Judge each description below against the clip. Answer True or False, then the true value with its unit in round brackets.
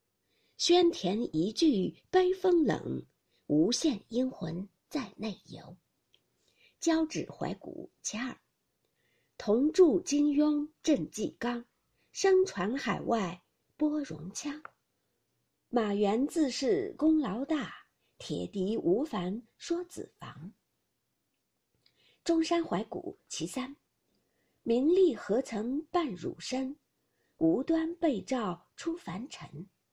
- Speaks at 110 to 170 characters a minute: True (135 characters per minute)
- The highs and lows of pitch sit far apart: True (6.8 semitones)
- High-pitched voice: True (290 Hz)